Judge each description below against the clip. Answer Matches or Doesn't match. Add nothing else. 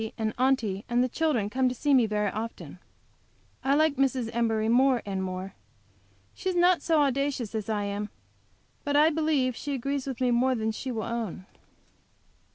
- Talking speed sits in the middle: Matches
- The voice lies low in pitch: Doesn't match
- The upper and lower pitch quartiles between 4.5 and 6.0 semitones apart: Doesn't match